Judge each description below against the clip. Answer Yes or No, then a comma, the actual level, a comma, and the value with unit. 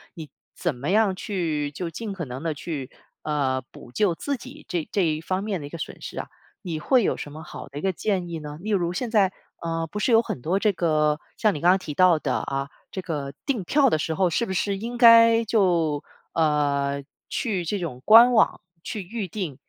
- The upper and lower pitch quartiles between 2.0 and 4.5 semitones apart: No, wide, 5.6 semitones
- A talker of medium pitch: Yes, medium, 175 Hz